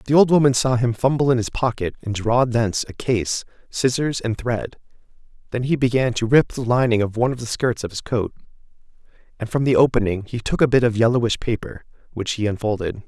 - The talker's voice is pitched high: No, low, 120 Hz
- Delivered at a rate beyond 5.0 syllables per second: Yes, 5.9 syllables/s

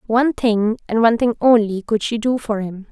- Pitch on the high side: Yes, high, 225 Hz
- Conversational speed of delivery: No, fast, 225 wpm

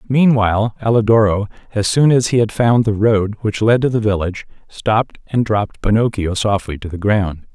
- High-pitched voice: No, low, 110 Hz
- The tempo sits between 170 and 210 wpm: Yes, average, 185 wpm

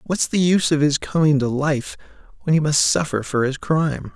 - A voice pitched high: No, medium, 145 Hz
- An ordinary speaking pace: No, fast, 215 wpm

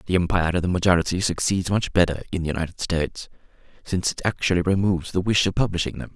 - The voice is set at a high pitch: No, very low, 90 Hz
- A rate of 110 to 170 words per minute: No, fast, 205 wpm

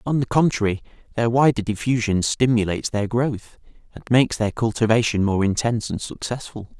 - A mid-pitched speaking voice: No, low, 115 Hz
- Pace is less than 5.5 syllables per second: No, 5.6 syllables/s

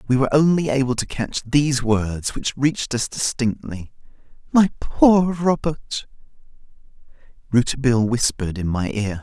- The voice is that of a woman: No, male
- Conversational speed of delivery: No, slow, 125 wpm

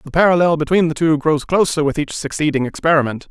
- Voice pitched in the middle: Yes, medium, 155 Hz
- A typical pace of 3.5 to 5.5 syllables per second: No, 6.1 syllables/s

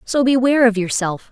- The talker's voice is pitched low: No, high, 235 Hz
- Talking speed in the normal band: Yes, average, 180 wpm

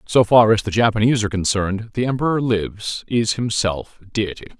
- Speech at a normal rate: Yes, average, 170 wpm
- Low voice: Yes, low, 110 Hz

